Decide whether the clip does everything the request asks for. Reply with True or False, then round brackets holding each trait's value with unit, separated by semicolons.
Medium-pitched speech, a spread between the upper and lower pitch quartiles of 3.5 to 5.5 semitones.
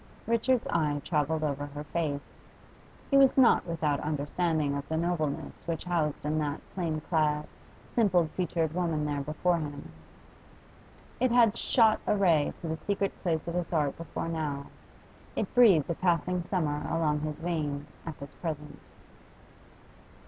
False (160 Hz; 3.1 semitones)